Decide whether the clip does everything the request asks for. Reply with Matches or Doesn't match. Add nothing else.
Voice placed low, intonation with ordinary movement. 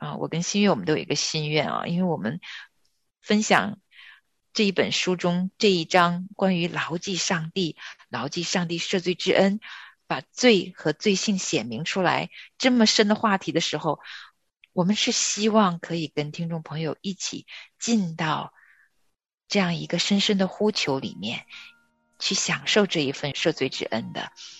Doesn't match